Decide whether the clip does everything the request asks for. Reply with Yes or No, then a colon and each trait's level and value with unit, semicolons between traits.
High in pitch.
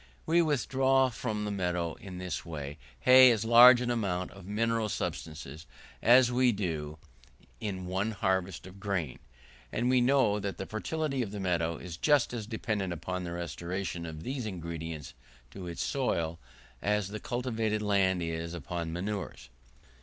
No: low, 100 Hz